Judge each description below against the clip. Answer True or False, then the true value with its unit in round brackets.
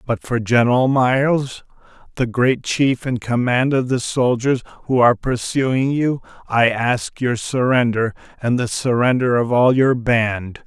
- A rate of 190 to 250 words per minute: False (150 wpm)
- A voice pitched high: False (125 Hz)